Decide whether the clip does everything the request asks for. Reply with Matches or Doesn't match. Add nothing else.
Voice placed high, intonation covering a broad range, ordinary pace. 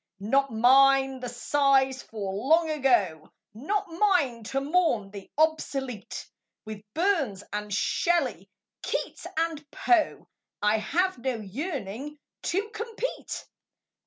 Doesn't match